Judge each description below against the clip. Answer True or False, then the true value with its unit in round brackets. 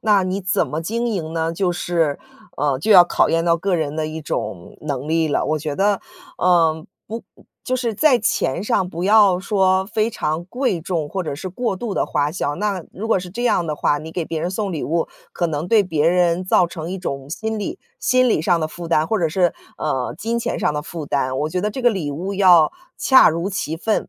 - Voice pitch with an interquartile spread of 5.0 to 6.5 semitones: False (4.1 semitones)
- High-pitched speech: False (175 Hz)